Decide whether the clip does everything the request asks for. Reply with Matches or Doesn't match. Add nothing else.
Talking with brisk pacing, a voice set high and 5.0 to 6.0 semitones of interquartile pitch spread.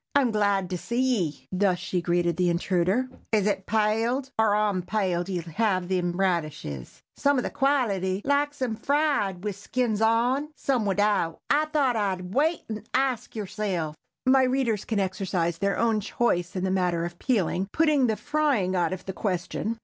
Doesn't match